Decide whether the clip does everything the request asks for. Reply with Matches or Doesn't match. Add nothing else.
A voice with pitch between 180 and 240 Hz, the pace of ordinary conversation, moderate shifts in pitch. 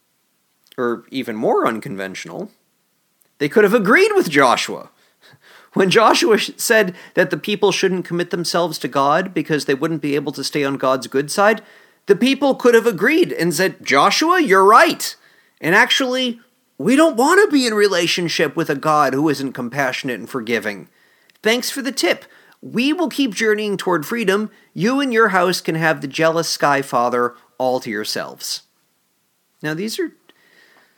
Doesn't match